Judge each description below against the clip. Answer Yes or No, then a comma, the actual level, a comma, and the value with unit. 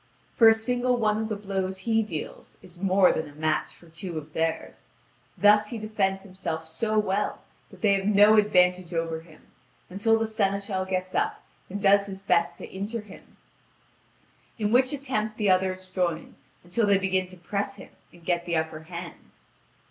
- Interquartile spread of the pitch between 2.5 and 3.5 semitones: Yes, average, 3.2 semitones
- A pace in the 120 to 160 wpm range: No, average, 180 wpm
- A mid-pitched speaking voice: No, high, 195 Hz